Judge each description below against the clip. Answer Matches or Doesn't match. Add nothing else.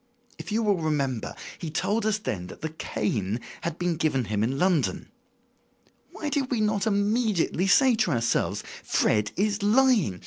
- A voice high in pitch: Doesn't match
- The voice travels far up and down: Matches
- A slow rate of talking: Doesn't match